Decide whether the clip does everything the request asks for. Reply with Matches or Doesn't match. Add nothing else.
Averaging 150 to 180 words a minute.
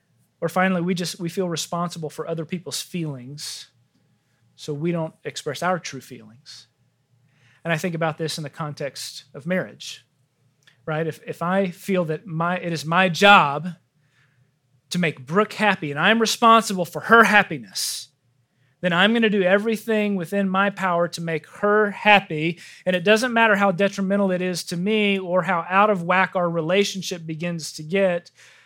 Matches